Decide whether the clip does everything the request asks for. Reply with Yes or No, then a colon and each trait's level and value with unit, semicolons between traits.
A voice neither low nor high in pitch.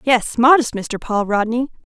No: high, 235 Hz